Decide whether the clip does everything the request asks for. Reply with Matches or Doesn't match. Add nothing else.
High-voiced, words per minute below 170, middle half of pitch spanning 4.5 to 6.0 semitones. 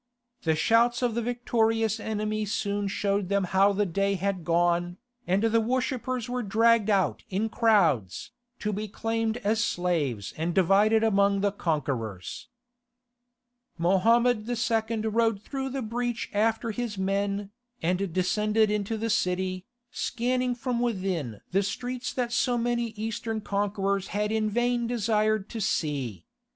Doesn't match